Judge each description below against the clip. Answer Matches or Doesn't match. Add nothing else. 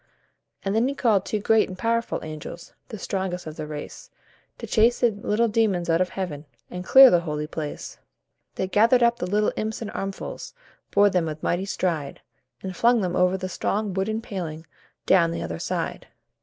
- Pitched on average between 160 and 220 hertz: Matches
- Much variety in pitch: Doesn't match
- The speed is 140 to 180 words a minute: Doesn't match